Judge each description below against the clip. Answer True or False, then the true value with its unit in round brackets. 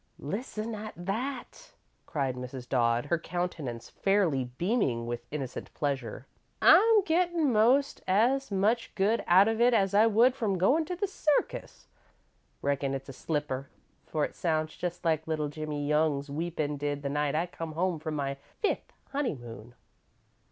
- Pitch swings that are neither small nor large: False (7.8 semitones)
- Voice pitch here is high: False (165 Hz)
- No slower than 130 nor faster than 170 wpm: True (155 wpm)